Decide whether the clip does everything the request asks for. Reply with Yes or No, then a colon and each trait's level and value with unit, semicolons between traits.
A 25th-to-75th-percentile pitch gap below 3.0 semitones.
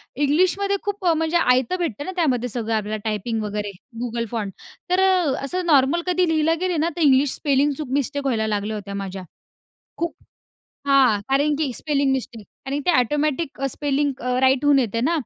No: average, 5.3 semitones